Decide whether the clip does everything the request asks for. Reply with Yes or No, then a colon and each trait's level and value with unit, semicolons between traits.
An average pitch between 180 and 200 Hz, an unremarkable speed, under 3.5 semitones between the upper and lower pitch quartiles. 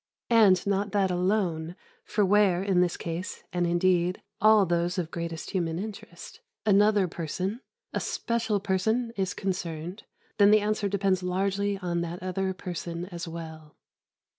Yes: medium, 185 Hz; average, 150 wpm; average, 2.7 semitones